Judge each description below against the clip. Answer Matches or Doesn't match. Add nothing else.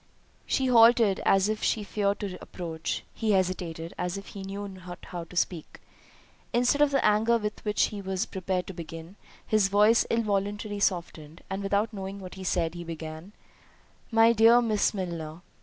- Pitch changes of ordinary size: Matches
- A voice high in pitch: Matches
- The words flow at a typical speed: Matches